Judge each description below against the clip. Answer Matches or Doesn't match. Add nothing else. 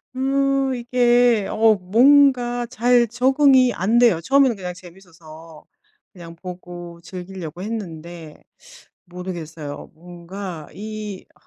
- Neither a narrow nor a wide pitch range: Doesn't match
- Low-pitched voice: Doesn't match